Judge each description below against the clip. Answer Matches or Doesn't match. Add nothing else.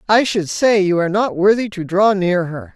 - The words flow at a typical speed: Doesn't match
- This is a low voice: Doesn't match